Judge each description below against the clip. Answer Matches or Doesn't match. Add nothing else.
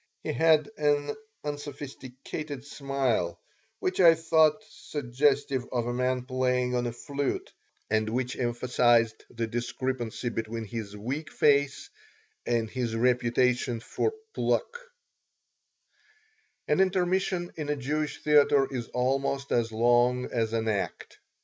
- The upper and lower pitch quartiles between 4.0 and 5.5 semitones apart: Doesn't match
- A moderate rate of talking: Doesn't match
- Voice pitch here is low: Matches